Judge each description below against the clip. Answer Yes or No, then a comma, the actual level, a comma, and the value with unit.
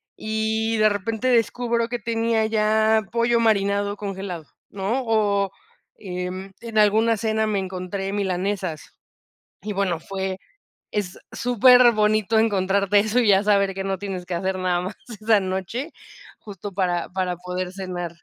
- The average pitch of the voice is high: Yes, high, 200 Hz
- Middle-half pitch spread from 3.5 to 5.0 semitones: No, average, 2.7 semitones